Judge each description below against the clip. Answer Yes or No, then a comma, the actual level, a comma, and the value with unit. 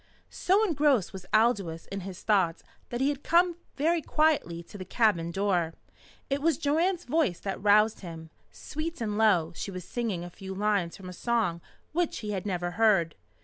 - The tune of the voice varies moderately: No, wide, 8.2 semitones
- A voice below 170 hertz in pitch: No, high, 210 Hz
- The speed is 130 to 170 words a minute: No, average, 185 wpm